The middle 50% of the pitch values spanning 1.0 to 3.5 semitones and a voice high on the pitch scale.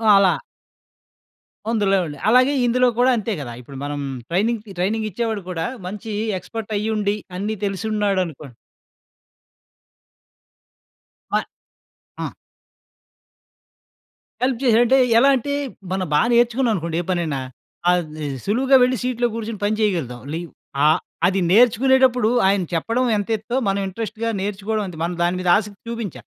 No: average, 4.3 semitones; high, 210 Hz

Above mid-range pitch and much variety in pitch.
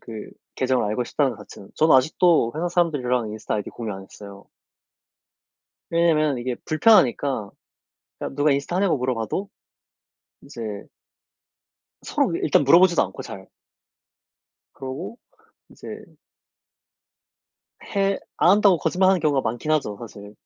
No: medium, 140 Hz; wide, 6.7 semitones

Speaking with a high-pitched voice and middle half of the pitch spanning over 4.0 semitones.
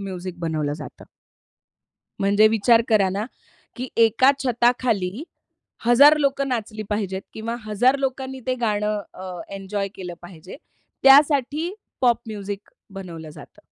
Yes: high, 215 Hz; average, 4.9 semitones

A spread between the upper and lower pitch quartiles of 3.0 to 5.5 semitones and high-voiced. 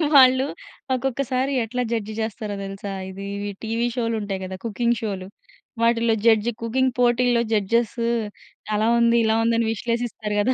No: narrow, 2.4 semitones; high, 230 Hz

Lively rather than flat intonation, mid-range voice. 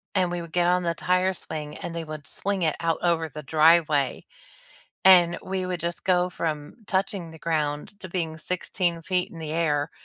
No: narrow, 2.4 semitones; medium, 170 Hz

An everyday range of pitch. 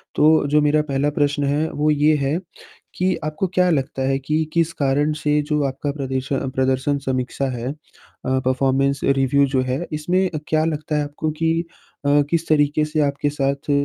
No: narrow, 2.1 semitones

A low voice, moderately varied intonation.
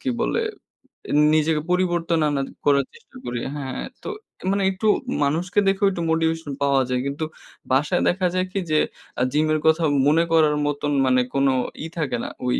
No: medium, 155 Hz; average, 4.0 semitones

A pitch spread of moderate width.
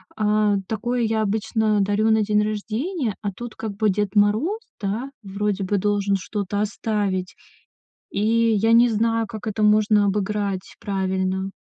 No: narrow, 1.6 semitones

